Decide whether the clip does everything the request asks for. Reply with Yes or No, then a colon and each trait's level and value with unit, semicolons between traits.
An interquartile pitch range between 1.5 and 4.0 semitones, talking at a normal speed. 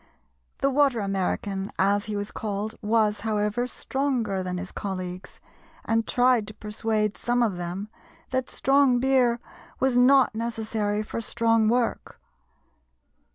No: average, 3.2 semitones; slow, 130 wpm